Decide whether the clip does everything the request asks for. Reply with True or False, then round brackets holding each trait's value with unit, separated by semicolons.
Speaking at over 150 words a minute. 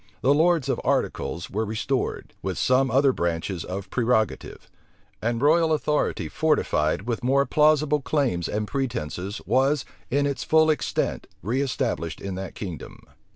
False (140 wpm)